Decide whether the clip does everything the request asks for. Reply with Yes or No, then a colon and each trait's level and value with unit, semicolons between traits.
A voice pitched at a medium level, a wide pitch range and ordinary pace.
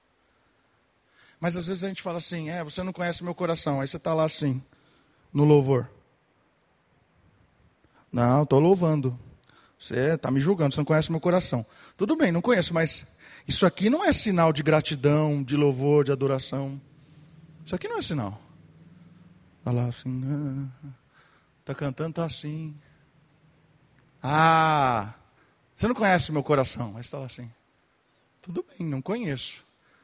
No: medium, 150 Hz; average, 3.7 semitones; average, 160 wpm